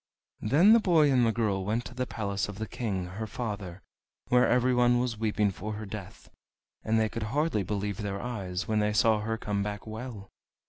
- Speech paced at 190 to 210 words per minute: Yes, average, 200 wpm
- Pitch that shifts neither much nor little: Yes, average, 3.0 semitones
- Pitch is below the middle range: Yes, low, 110 Hz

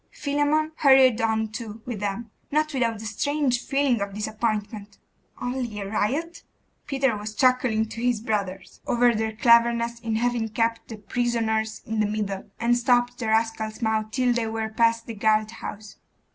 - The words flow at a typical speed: Yes, average, 165 wpm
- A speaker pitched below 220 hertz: No, high, 230 Hz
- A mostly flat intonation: Yes, narrow, 2.2 semitones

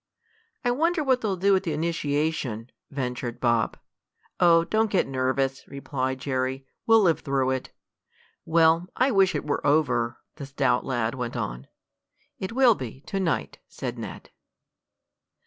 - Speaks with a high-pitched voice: No, medium, 145 Hz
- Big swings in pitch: Yes, wide, 6.4 semitones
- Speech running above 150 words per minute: No, average, 145 wpm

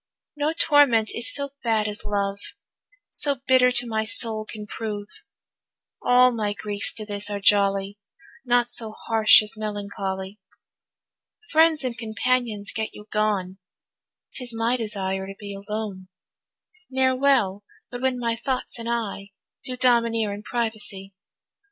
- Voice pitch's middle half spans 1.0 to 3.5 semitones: Yes, average, 3.1 semitones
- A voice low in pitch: No, high, 220 Hz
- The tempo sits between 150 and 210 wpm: No, average, 140 wpm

